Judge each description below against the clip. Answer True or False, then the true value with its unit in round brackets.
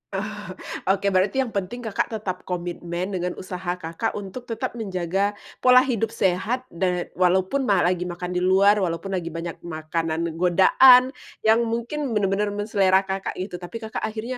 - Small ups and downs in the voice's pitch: False (3.8 semitones)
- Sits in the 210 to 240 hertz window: False (195 Hz)